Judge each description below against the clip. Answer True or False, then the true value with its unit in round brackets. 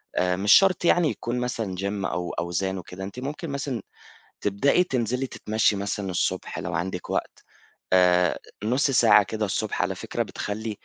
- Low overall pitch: True (105 Hz)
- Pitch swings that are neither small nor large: True (5.0 semitones)